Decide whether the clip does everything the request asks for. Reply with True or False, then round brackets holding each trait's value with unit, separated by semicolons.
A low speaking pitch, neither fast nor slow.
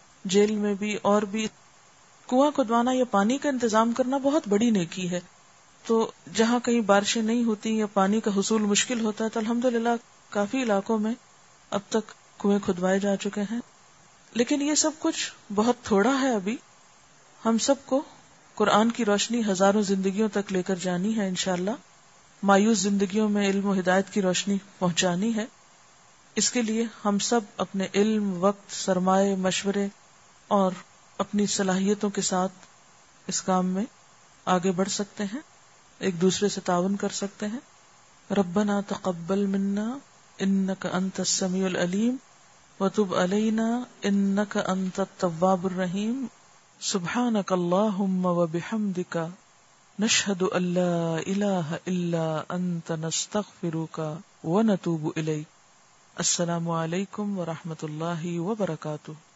False (200 Hz; 135 wpm)